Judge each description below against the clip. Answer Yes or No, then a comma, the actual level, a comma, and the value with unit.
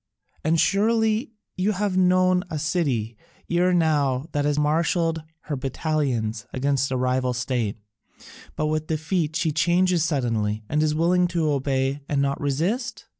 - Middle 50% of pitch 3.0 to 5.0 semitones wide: Yes, average, 4.6 semitones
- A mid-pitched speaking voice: Yes, medium, 155 Hz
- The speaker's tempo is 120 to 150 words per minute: Yes, average, 145 wpm